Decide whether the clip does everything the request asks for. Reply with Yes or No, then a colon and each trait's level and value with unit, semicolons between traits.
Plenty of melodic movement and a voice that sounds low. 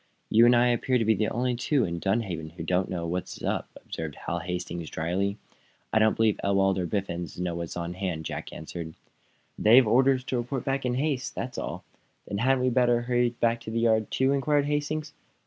Yes: wide, 5.9 semitones; low, 110 Hz